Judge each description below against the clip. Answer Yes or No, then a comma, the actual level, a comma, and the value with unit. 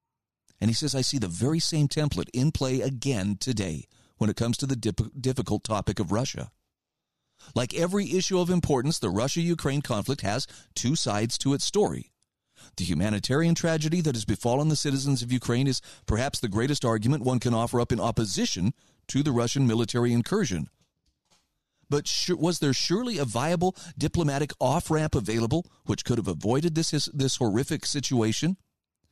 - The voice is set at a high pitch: No, low, 130 Hz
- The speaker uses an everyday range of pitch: Yes, average, 4.9 semitones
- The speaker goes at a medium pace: Yes, average, 170 wpm